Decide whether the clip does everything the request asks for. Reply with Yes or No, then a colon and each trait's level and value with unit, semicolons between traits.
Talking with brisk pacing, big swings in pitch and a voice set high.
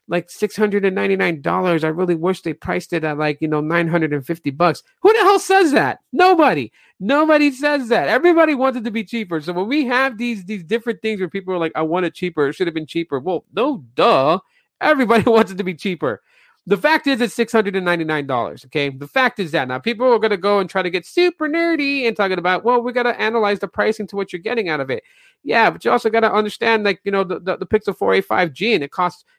Yes: fast, 240 wpm; wide, 5.8 semitones; high, 205 Hz